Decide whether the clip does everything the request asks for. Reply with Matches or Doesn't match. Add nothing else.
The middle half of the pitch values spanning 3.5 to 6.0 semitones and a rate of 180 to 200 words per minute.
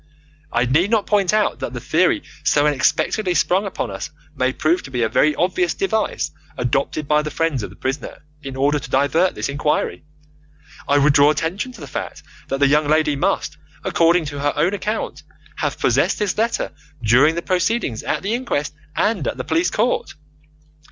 Matches